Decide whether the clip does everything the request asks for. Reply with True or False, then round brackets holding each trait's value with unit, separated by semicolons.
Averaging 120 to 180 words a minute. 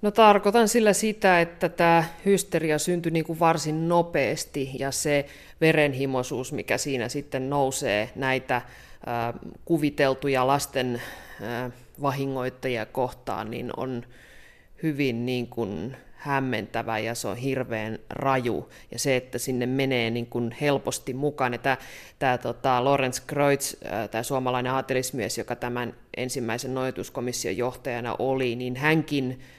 True (130 wpm)